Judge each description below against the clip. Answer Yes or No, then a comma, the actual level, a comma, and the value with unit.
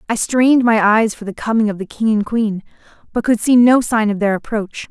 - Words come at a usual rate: No, fast, 245 wpm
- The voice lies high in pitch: Yes, high, 220 Hz